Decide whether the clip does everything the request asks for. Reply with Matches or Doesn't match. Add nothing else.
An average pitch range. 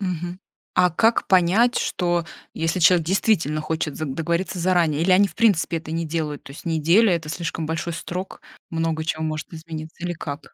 Doesn't match